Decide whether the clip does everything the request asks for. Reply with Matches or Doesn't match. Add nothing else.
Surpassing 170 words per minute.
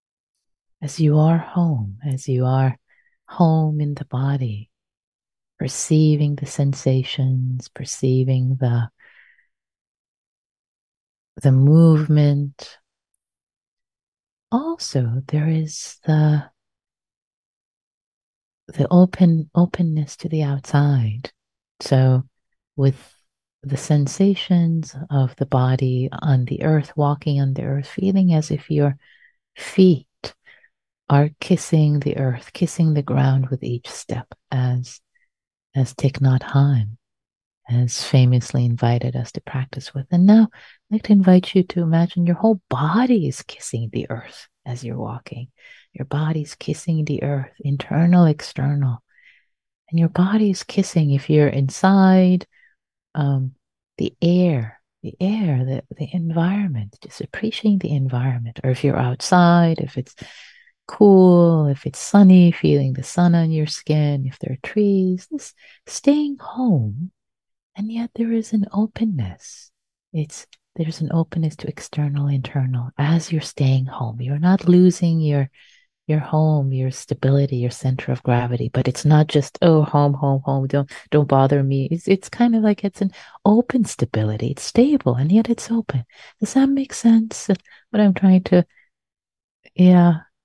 Doesn't match